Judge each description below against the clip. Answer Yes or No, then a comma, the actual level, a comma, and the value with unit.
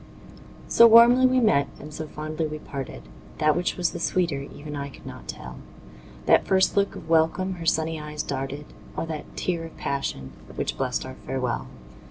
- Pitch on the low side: No, medium, 155 Hz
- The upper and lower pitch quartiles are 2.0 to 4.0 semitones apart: Yes, average, 3.7 semitones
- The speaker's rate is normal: Yes, average, 185 wpm